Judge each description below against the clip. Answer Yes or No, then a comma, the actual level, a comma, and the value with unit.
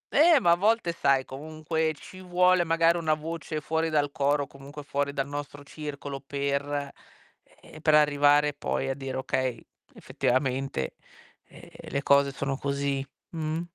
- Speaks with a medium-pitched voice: Yes, medium, 145 Hz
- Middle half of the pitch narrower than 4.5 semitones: Yes, narrow, 2.4 semitones